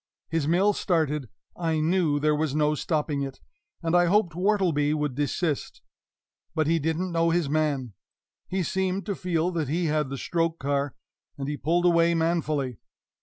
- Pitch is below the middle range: No, medium, 160 Hz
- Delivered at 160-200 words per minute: Yes, average, 170 wpm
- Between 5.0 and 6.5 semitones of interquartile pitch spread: No, average, 2.8 semitones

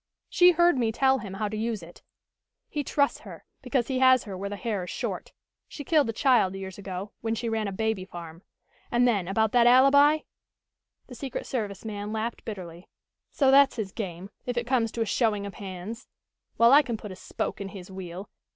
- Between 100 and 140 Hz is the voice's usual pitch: No, high, 220 Hz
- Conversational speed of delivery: No, fast, 215 wpm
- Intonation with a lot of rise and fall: No, average, 4.6 semitones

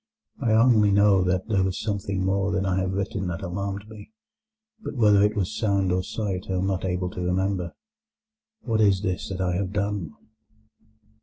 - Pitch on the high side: No, very low, 95 Hz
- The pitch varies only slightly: Yes, narrow, 1.9 semitones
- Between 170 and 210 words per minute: Yes, average, 185 wpm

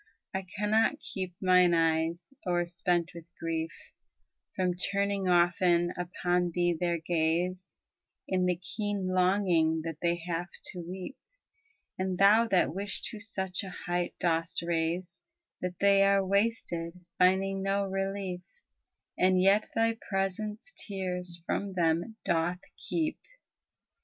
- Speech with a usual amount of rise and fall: No, narrow, 2.3 semitones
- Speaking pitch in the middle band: Yes, medium, 180 Hz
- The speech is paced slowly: Yes, slow, 125 wpm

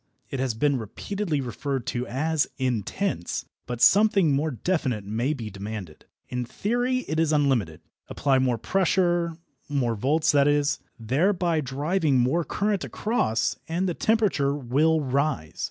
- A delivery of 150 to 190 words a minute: No, average, 140 wpm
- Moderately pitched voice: Yes, medium, 145 Hz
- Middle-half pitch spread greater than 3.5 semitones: Yes, wide, 5.5 semitones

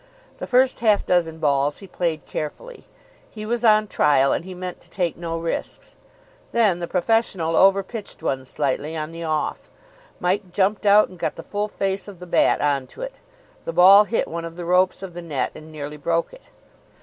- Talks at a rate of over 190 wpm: Yes, average, 200 wpm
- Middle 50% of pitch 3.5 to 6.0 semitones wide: Yes, average, 4.1 semitones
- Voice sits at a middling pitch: Yes, medium, 180 Hz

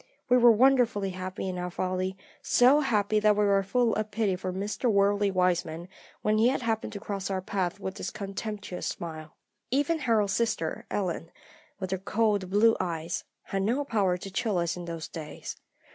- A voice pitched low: No, high, 200 Hz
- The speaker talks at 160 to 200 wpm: Yes, average, 180 wpm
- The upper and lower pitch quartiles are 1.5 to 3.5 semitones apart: Yes, average, 3.2 semitones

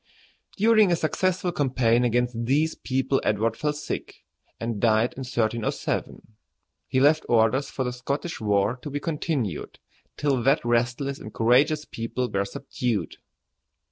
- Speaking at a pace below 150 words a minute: Yes, average, 140 wpm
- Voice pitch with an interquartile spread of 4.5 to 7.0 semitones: No, average, 4.1 semitones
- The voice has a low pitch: Yes, low, 125 Hz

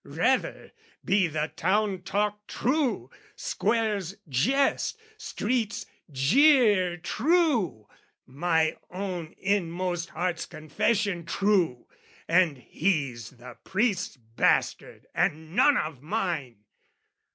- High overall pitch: No, medium, 180 Hz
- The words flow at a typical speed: No, slow, 90 wpm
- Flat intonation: No, average, 5.2 semitones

